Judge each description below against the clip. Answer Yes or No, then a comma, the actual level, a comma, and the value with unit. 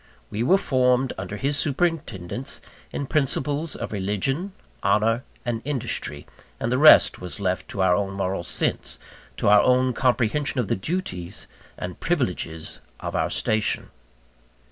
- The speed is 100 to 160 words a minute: Yes, average, 145 wpm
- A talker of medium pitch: No, low, 120 Hz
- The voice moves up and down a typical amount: No, wide, 6.3 semitones